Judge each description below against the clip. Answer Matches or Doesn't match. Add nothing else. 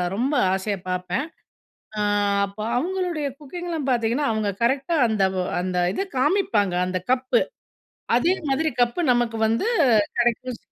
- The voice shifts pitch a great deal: Matches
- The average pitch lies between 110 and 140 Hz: Doesn't match